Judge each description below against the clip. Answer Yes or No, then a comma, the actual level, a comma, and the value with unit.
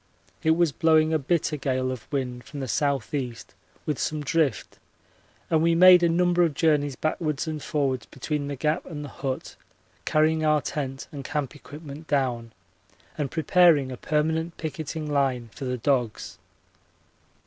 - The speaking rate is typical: Yes, average, 160 wpm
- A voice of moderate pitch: Yes, medium, 150 Hz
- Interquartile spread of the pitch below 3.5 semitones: Yes, average, 3.0 semitones